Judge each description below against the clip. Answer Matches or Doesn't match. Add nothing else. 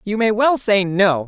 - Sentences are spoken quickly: Matches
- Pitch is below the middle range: Doesn't match